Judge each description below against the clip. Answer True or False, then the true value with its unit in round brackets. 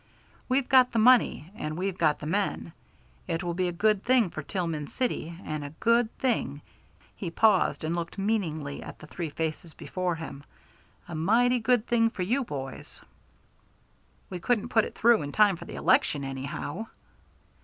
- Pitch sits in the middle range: True (180 Hz)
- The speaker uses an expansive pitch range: True (6.3 semitones)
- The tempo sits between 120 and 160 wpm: False (175 wpm)